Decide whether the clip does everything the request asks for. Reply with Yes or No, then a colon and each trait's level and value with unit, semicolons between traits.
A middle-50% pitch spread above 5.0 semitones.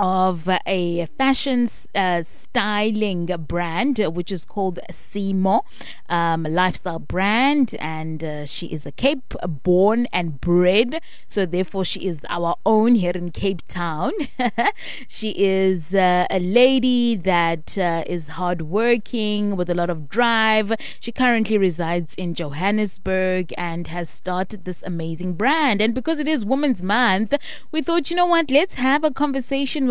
Yes: wide, 5.5 semitones